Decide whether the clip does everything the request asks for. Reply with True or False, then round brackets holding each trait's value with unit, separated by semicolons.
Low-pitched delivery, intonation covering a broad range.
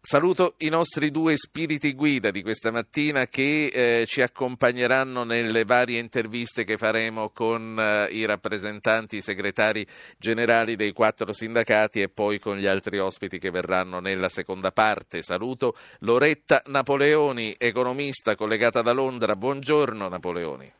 False (115 Hz; 4.1 semitones)